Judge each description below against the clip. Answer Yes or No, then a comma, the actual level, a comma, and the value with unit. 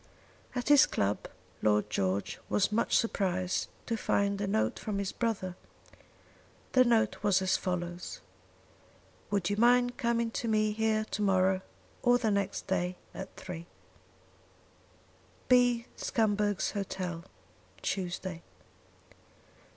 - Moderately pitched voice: No, high, 200 Hz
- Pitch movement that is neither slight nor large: Yes, average, 3.6 semitones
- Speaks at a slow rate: Yes, slow, 120 wpm